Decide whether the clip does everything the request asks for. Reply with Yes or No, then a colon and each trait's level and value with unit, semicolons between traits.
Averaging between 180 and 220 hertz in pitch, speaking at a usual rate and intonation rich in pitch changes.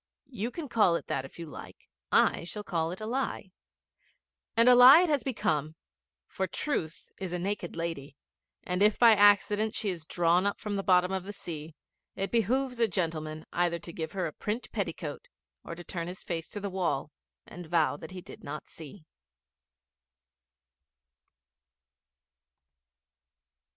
No: medium, 185 Hz; average, 165 wpm; average, 4.2 semitones